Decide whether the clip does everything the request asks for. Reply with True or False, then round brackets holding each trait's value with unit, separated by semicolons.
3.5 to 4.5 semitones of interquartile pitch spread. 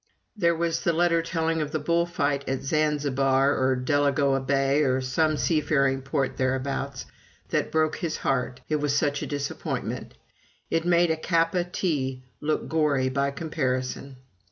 False (3.1 semitones)